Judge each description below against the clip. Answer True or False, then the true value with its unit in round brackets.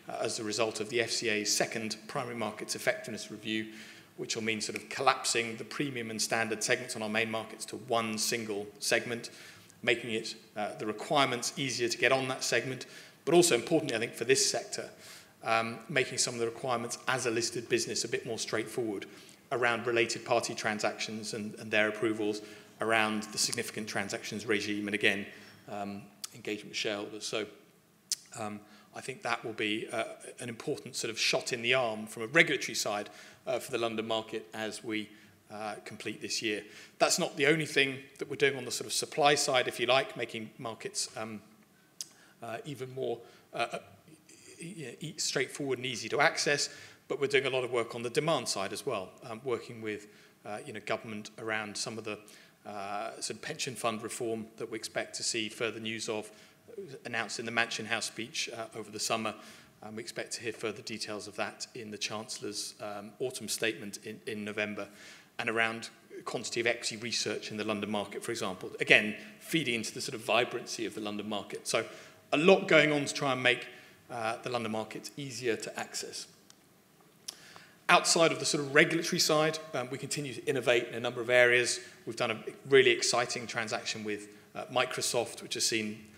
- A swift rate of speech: False (195 wpm)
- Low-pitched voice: True (115 Hz)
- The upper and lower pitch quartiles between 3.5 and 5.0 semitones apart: False (2.7 semitones)